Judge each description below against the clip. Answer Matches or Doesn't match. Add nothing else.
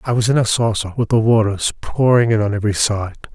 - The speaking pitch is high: Doesn't match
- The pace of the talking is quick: Matches